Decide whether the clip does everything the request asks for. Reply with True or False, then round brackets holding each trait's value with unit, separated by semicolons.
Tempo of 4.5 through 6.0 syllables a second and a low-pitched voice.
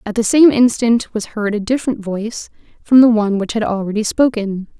False (5.6 syllables/s; 220 Hz)